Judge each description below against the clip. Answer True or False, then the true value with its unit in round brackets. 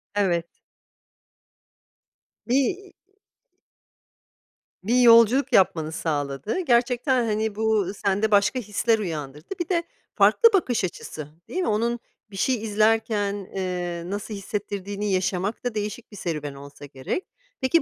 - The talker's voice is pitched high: True (210 Hz)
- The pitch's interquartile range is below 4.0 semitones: False (4.6 semitones)